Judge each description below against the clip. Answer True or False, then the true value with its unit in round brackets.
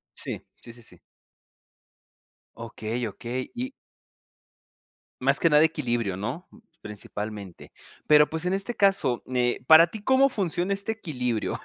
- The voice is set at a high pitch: False (150 Hz)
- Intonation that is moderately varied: False (8.6 semitones)